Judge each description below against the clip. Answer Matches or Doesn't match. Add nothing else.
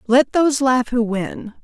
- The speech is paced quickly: Doesn't match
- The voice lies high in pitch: Matches